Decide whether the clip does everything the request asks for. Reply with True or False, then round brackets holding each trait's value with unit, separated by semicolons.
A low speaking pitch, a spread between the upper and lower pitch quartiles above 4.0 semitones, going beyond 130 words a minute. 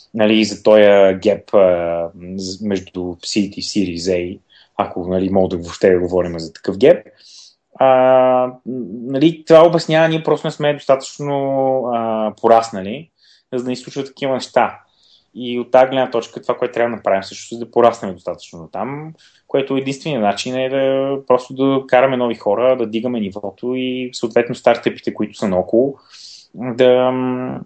True (120 Hz; 4.7 semitones; 155 wpm)